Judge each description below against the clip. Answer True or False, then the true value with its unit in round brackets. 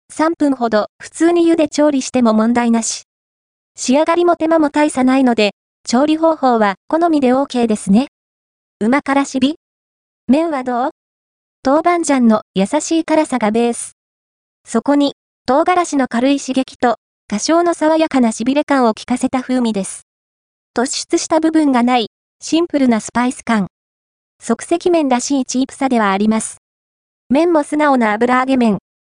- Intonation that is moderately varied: True (5.0 semitones)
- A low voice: False (260 Hz)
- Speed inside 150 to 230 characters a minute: False (290 characters per minute)